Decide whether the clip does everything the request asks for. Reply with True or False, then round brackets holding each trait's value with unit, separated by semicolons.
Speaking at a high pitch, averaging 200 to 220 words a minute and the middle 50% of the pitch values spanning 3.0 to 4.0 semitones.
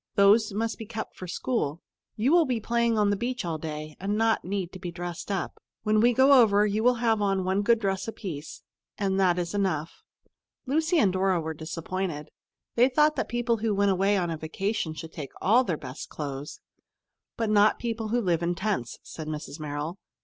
False (200 Hz; 205 wpm; 5.0 semitones)